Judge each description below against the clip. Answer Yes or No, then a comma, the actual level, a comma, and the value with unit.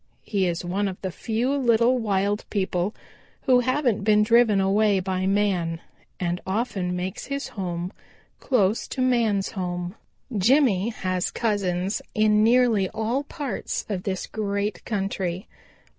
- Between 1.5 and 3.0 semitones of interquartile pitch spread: No, average, 3.6 semitones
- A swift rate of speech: No, average, 140 wpm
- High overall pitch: Yes, high, 205 Hz